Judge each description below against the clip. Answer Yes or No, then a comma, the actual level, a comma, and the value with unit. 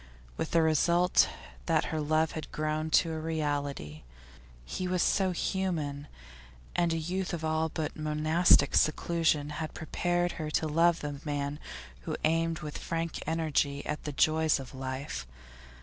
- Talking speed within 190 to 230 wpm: No, average, 150 wpm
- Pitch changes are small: Yes, narrow, 2.0 semitones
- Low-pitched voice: No, medium, 155 Hz